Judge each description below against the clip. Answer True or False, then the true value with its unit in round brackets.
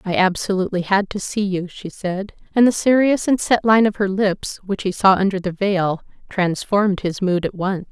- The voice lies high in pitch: True (195 Hz)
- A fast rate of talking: True (210 wpm)